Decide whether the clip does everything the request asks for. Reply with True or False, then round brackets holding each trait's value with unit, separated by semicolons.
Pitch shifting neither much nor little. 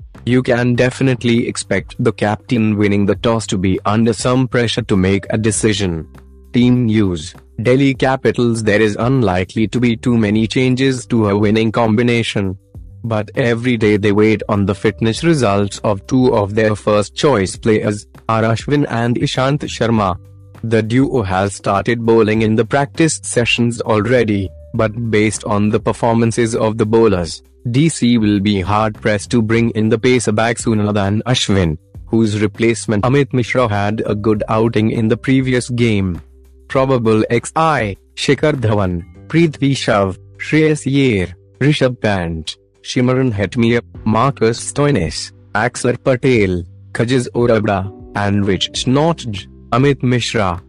True (3.4 semitones)